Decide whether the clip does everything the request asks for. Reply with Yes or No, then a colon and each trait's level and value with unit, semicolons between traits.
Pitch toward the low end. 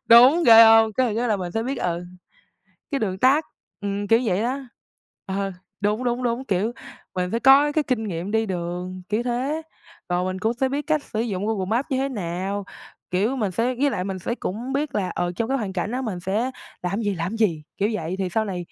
No: high, 215 Hz